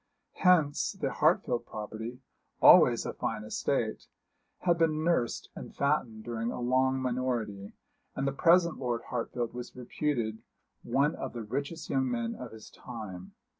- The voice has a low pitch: Yes, low, 125 Hz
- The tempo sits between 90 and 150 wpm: Yes, average, 145 wpm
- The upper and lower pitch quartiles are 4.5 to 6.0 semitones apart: No, average, 3.9 semitones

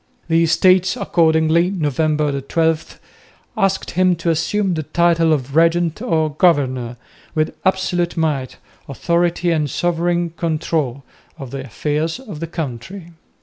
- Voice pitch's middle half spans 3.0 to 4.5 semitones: No, narrow, 2.5 semitones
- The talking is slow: Yes, slow, 125 wpm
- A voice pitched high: No, medium, 165 Hz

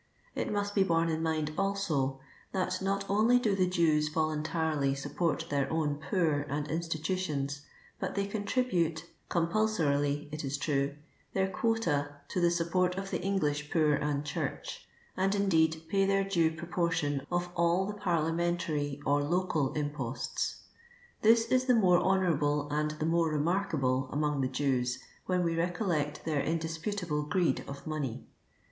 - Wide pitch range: No, average, 4.1 semitones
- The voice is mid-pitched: Yes, medium, 165 Hz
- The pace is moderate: Yes, average, 155 wpm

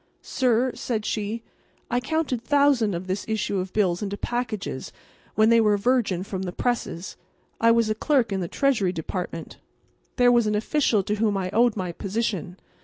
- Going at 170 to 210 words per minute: Yes, average, 180 wpm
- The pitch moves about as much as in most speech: Yes, average, 4.0 semitones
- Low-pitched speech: No, high, 215 Hz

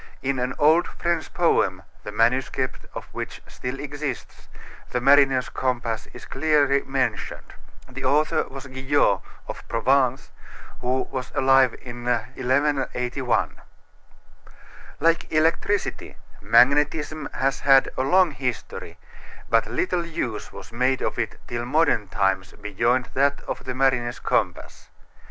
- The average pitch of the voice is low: Yes, low, 130 Hz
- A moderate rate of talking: No, slow, 125 wpm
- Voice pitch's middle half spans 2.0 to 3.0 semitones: Yes, average, 2.7 semitones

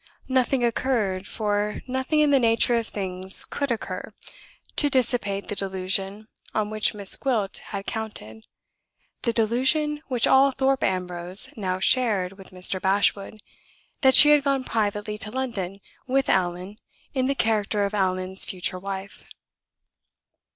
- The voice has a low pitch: No, high, 210 Hz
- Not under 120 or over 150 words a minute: Yes, average, 140 wpm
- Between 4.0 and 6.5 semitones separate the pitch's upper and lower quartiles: Yes, average, 5.0 semitones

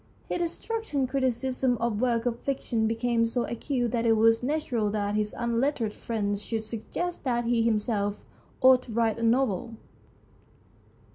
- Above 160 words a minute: No, average, 155 wpm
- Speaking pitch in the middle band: No, high, 235 Hz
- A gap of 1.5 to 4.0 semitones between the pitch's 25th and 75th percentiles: Yes, narrow, 2.5 semitones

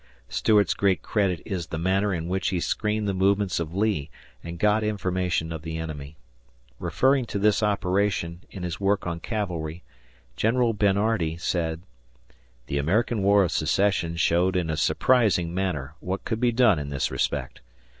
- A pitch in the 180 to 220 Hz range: No, very low, 95 Hz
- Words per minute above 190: No, average, 160 wpm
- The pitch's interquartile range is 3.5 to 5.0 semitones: Yes, average, 3.8 semitones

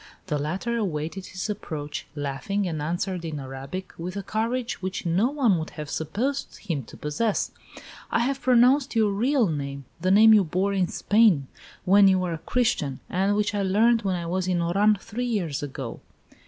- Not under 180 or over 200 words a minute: Yes, average, 185 wpm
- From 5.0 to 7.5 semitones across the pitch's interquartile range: Yes, wide, 5.5 semitones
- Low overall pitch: No, high, 190 Hz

